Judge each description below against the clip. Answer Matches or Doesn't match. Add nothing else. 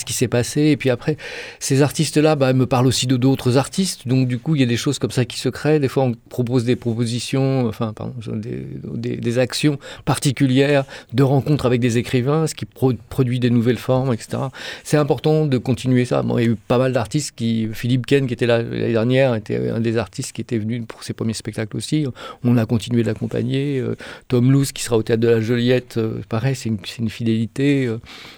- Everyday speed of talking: Doesn't match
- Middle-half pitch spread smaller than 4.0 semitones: Matches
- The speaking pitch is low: Matches